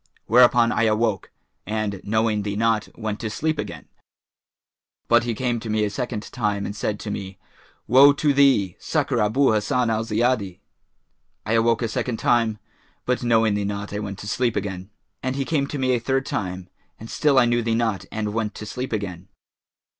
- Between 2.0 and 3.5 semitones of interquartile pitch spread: Yes, average, 2.9 semitones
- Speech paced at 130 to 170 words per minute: No, average, 190 wpm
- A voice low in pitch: Yes, low, 110 Hz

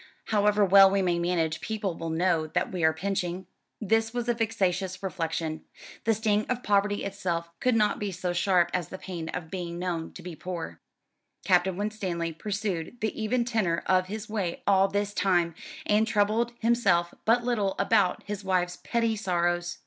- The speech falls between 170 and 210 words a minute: Yes, average, 175 wpm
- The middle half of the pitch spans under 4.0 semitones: Yes, average, 3.4 semitones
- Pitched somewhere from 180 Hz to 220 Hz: Yes, high, 190 Hz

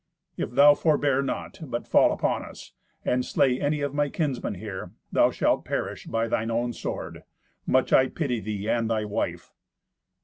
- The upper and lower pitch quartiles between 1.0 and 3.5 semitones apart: No, average, 4.0 semitones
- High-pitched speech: No, low, 125 Hz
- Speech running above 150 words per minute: Yes, average, 170 wpm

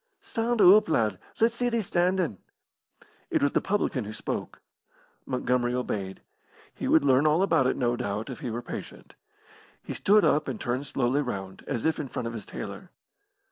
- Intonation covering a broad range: Yes, wide, 6.8 semitones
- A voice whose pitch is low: Yes, low, 130 Hz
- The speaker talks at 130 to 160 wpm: No, average, 180 wpm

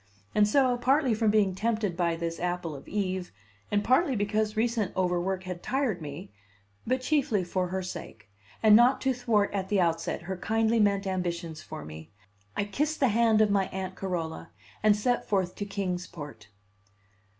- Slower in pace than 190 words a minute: Yes, average, 175 wpm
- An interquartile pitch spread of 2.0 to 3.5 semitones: No, average, 3.9 semitones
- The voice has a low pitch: No, high, 200 Hz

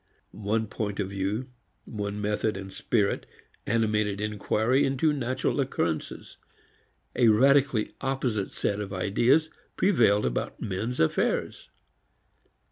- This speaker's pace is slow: Yes, slow, 110 wpm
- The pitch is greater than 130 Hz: No, low, 110 Hz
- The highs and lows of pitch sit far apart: No, average, 4.2 semitones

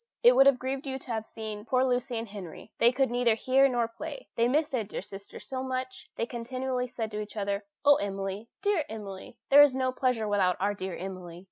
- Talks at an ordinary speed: No, fast, 225 wpm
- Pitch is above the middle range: Yes, high, 235 Hz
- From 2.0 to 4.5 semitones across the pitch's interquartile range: Yes, average, 4.1 semitones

